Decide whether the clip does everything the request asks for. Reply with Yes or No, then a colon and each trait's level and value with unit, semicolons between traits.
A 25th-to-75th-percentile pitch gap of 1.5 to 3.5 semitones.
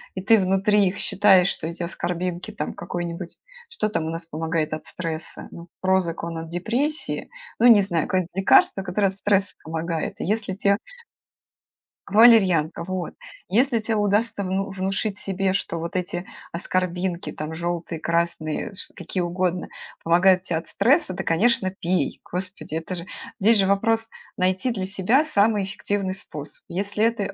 Yes: average, 3.0 semitones